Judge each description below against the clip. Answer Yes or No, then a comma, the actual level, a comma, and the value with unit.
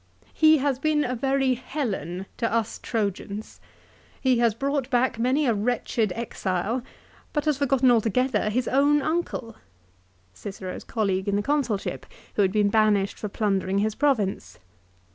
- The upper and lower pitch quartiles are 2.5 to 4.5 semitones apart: No, average, 4.9 semitones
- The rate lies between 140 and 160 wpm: Yes, average, 155 wpm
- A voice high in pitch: Yes, high, 230 Hz